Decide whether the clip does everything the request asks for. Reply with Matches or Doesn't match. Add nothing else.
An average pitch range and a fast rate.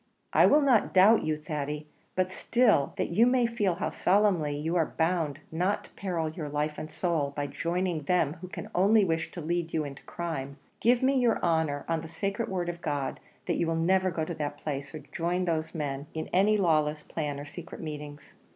Matches